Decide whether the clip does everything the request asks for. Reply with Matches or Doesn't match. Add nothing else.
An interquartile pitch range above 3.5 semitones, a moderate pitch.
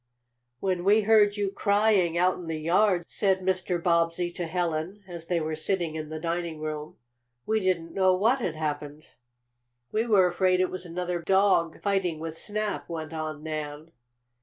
Doesn't match